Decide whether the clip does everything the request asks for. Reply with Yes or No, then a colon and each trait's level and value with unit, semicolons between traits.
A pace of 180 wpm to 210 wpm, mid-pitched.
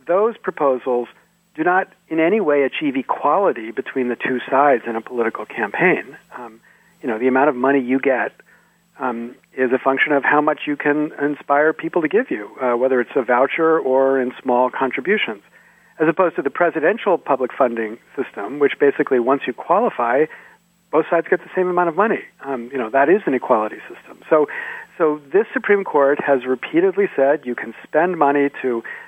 Yes: average, 190 wpm; medium, 145 Hz